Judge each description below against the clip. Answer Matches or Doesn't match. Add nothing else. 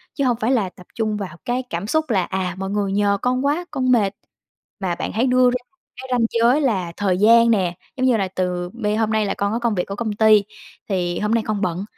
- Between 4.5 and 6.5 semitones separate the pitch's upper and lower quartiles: Doesn't match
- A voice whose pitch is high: Matches